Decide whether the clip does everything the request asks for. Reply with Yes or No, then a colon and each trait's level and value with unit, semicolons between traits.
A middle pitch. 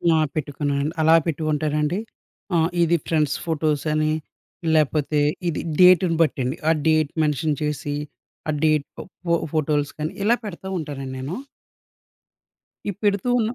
Yes: medium, 155 Hz